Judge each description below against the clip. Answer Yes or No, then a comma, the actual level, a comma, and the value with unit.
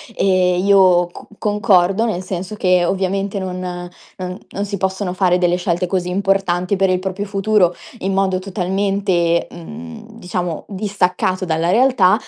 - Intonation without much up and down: Yes, narrow, 1.7 semitones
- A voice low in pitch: No, medium, 185 Hz